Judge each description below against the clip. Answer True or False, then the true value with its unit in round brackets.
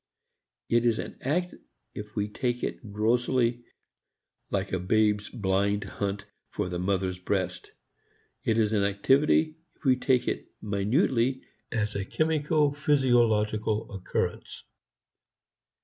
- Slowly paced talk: True (120 wpm)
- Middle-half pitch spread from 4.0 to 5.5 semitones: True (4.3 semitones)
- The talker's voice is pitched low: True (110 Hz)